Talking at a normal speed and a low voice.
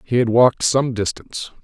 Yes: average, 185 wpm; low, 120 Hz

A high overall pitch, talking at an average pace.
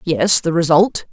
No: medium, 170 Hz; average, 160 wpm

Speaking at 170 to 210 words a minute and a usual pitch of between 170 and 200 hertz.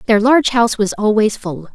No: fast, 205 wpm; high, 220 Hz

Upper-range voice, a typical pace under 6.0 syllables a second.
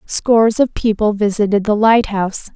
Yes: high, 210 Hz; 5.0 syllables/s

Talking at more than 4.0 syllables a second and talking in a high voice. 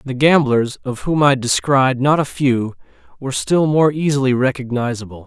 No: 4.9 syllables/s; low, 135 Hz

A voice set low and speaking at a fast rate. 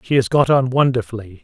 Yes: low, 125 Hz; fast, 210 wpm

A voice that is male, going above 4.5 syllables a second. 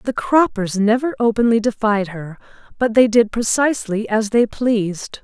No: female; 4.7 syllables/s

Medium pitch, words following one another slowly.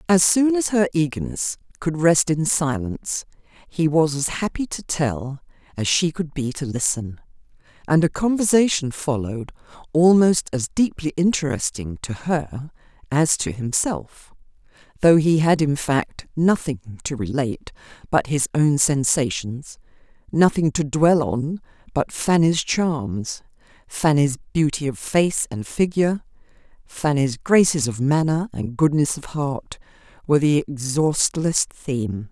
Yes: medium, 150 Hz; slow, 130 wpm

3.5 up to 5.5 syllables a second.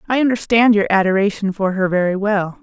No: 5.7 syllables/s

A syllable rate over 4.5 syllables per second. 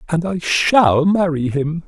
No: 3.6 syllables/s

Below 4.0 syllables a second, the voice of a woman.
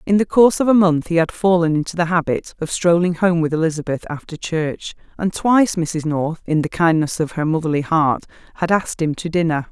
No: 5.6 syllables/s; female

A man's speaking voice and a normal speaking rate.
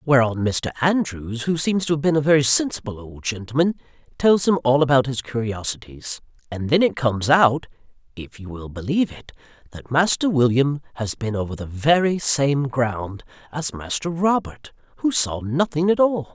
Yes: male; average, 165 wpm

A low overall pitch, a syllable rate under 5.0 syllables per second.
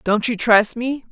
No: high, 230 Hz; 4.1 syllables/s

